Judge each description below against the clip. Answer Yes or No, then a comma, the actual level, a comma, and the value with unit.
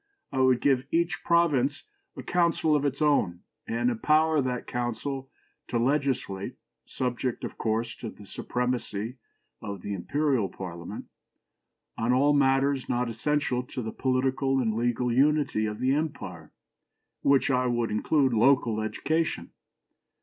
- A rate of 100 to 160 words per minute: Yes, average, 140 wpm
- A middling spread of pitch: Yes, average, 3.6 semitones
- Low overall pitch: Yes, low, 130 Hz